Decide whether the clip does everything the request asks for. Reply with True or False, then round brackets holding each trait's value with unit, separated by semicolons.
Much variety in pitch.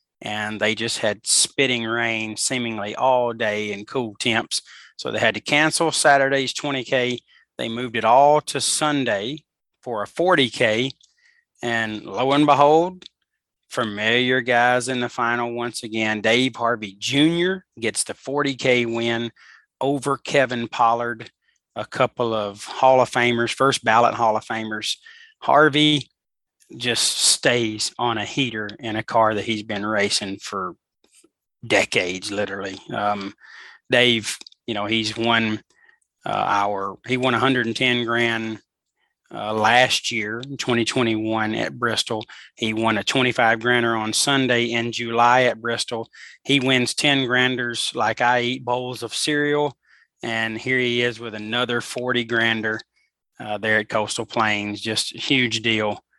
False (2.9 semitones)